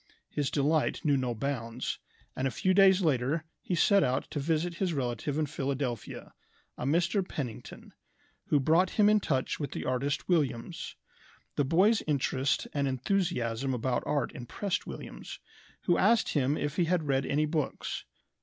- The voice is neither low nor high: Yes, medium, 145 Hz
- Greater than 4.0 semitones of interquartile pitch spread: Yes, average, 4.7 semitones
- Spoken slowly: No, average, 160 wpm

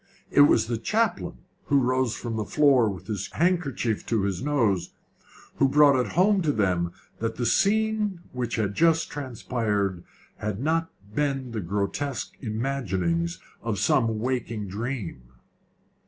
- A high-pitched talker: No, low, 120 Hz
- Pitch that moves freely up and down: Yes, wide, 5.8 semitones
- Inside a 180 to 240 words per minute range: No, average, 140 wpm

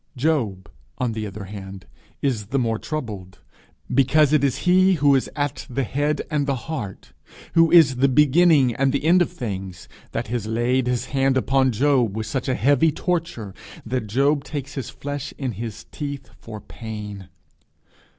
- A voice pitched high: No, low, 130 Hz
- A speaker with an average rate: Yes, average, 170 wpm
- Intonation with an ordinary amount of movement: Yes, average, 4.5 semitones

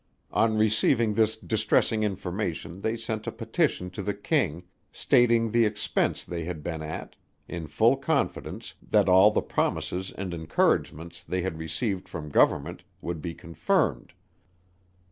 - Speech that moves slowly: No, average, 145 wpm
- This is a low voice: Yes, very low, 95 Hz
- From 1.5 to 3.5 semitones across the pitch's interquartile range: No, average, 4.5 semitones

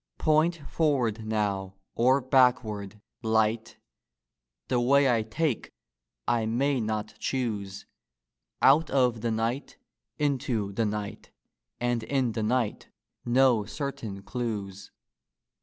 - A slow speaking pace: Yes, slow, 110 wpm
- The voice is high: No, low, 115 Hz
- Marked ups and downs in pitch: No, average, 3.5 semitones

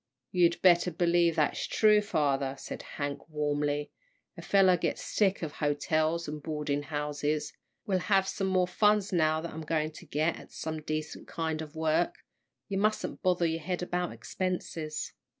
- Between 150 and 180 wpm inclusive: Yes, average, 165 wpm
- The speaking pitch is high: No, medium, 160 Hz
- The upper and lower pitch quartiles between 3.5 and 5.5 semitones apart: No, average, 3.0 semitones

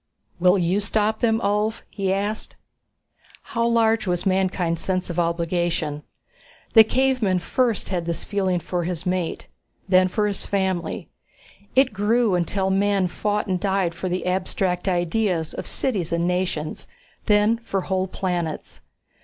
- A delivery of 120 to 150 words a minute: Yes, average, 145 wpm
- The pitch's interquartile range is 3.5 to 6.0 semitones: No, average, 2.8 semitones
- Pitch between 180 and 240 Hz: Yes, high, 190 Hz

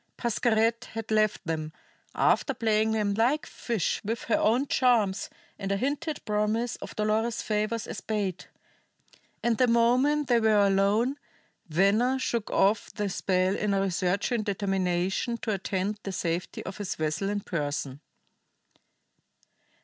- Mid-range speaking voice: No, high, 210 Hz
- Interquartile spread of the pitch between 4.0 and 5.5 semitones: No, average, 3.1 semitones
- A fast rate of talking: No, average, 140 wpm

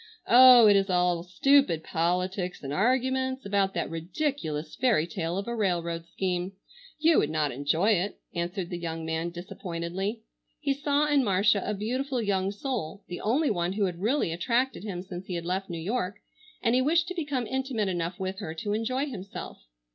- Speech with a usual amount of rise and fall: No, wide, 6.4 semitones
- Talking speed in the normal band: Yes, average, 185 wpm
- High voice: Yes, high, 195 Hz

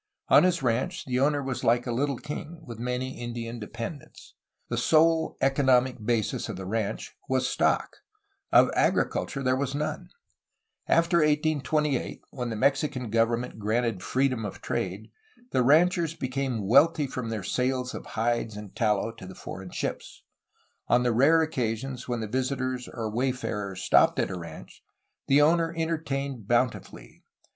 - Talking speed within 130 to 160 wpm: Yes, average, 150 wpm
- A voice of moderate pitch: No, low, 125 Hz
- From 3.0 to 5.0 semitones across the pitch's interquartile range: Yes, average, 3.8 semitones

